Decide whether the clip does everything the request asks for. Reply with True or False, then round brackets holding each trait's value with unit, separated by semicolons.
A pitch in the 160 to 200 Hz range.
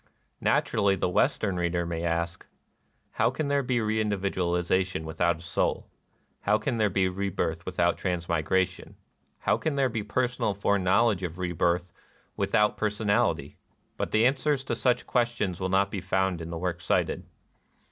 False (95 Hz)